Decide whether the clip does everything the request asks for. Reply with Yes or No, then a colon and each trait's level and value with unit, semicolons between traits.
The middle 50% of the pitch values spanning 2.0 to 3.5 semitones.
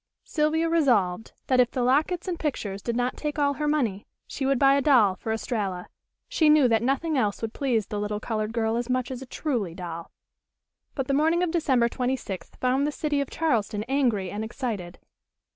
No: average, 5.1 semitones